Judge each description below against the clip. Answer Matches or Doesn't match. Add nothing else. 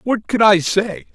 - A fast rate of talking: Matches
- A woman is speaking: Doesn't match